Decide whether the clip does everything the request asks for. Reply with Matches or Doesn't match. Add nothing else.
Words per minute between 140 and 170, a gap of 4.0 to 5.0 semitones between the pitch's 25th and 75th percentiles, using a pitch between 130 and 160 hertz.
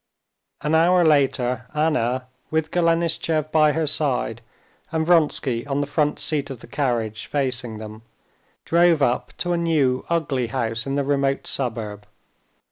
Matches